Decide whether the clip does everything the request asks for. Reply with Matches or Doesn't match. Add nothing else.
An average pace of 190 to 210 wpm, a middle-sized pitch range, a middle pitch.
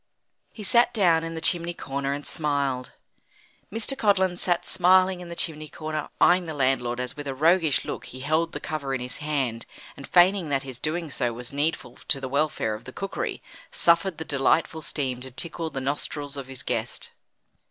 Matches